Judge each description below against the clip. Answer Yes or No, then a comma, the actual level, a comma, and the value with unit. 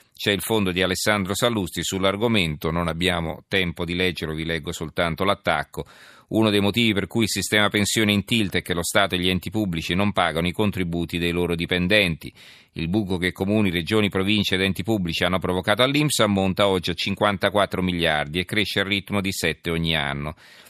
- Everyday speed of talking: No, fast, 190 wpm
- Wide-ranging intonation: No, average, 3.1 semitones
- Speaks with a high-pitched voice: No, very low, 95 Hz